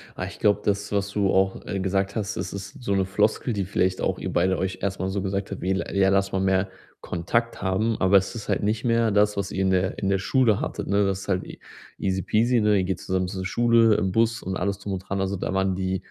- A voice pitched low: Yes, low, 100 Hz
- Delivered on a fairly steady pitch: Yes, narrow, 1.6 semitones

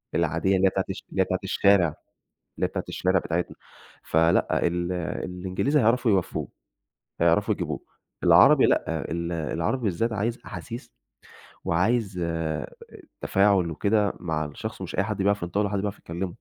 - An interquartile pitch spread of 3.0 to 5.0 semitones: Yes, average, 3.3 semitones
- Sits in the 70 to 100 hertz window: Yes, very low, 95 Hz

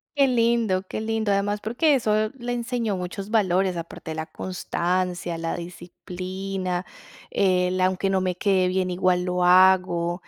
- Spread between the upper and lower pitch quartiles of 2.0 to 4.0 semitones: Yes, average, 2.8 semitones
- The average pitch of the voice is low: No, medium, 185 Hz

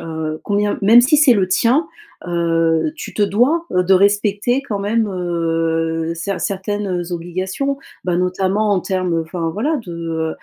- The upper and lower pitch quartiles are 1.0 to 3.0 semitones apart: No, average, 3.9 semitones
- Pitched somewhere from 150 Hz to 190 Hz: Yes, medium, 185 Hz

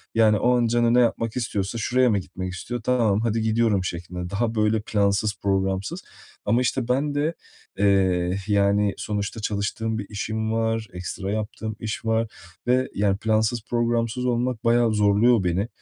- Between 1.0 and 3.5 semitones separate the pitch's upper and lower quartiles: Yes, average, 2.8 semitones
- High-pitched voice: No, low, 110 Hz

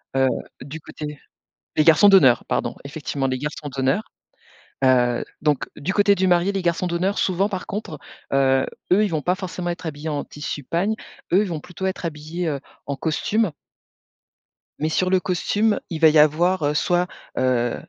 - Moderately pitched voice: Yes, medium, 160 Hz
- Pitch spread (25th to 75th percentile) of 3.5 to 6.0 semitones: Yes, average, 4.2 semitones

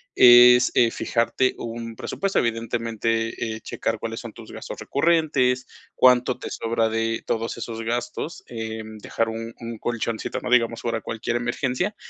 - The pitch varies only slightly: Yes, narrow, 1.5 semitones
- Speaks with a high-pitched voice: No, low, 115 Hz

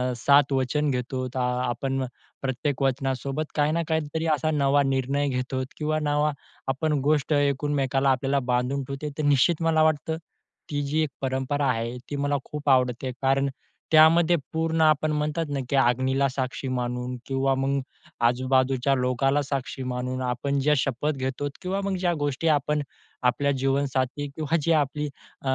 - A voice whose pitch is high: No, medium, 140 Hz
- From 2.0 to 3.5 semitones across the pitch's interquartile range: Yes, narrow, 2.4 semitones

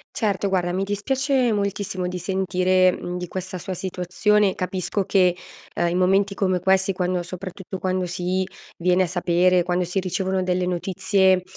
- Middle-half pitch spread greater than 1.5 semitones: No, narrow, 1.2 semitones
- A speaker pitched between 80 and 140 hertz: No, medium, 185 Hz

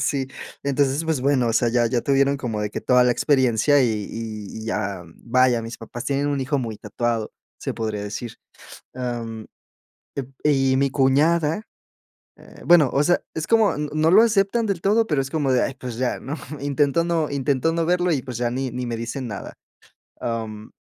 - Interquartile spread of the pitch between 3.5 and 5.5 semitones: Yes, average, 4.1 semitones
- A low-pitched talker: Yes, low, 130 Hz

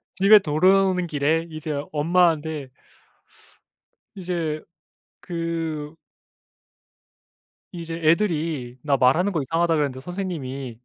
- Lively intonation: No, average, 3.0 semitones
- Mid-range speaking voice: Yes, medium, 160 Hz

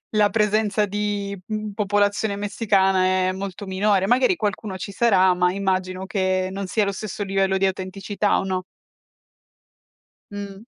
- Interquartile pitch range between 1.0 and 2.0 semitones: Yes, narrow, 1.6 semitones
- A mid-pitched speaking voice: No, high, 200 Hz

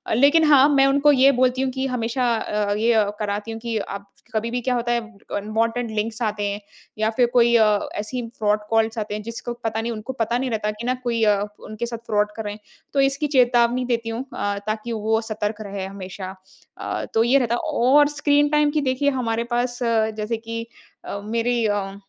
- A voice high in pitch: Yes, high, 230 Hz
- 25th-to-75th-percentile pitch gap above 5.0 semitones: No, average, 2.7 semitones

